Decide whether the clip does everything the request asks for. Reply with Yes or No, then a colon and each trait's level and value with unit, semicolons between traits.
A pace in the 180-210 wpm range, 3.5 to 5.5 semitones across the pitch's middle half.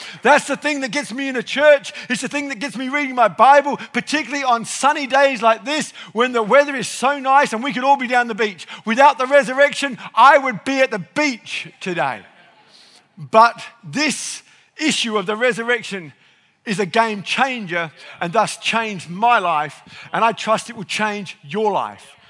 Yes: average, 190 wpm; average, 4.8 semitones